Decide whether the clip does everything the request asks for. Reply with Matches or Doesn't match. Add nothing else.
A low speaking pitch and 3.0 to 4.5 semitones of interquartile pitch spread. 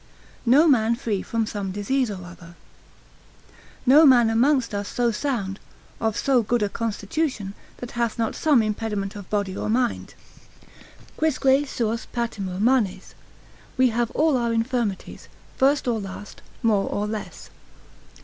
Doesn't match